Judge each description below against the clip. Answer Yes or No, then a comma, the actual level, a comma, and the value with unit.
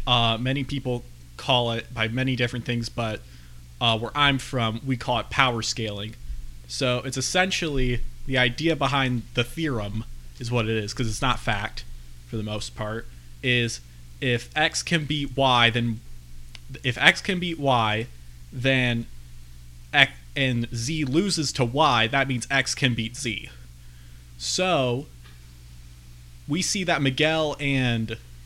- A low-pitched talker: Yes, low, 120 Hz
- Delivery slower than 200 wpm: Yes, average, 150 wpm